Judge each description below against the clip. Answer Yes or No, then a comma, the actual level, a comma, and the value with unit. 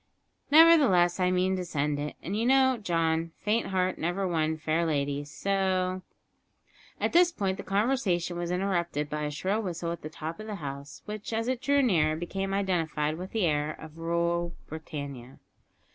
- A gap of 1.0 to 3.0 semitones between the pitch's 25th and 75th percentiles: No, average, 4.0 semitones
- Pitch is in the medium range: Yes, medium, 175 Hz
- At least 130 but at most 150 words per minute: No, average, 180 wpm